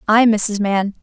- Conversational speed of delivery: Yes, average, 175 wpm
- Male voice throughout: No, female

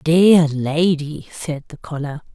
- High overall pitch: No, medium, 155 Hz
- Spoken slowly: Yes, slow, 130 wpm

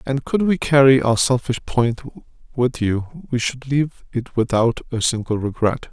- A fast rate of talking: No, average, 170 wpm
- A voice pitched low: Yes, low, 125 Hz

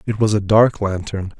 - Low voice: Yes, low, 105 Hz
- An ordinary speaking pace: No, fast, 215 wpm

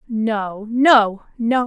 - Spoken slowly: Yes, slow, 110 wpm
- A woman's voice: Yes, female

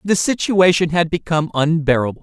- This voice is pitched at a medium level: Yes, medium, 165 Hz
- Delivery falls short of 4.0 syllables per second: No, 5.7 syllables/s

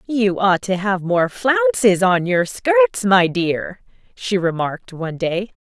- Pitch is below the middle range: No, high, 200 Hz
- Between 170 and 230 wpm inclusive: No, average, 160 wpm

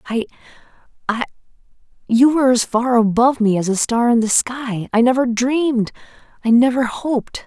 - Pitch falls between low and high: No, high, 240 Hz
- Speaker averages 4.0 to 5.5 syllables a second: Yes, 5.4 syllables/s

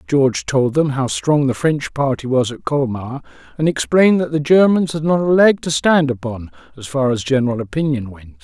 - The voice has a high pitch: No, low, 135 Hz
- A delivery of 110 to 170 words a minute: No, fast, 205 wpm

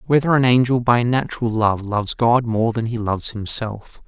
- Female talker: No, male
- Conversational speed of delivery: Yes, average, 190 wpm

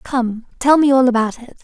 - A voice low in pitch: No, very high, 250 Hz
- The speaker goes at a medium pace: No, fast, 220 wpm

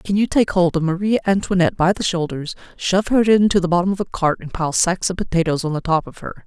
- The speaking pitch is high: No, medium, 180 Hz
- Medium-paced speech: No, fast, 260 wpm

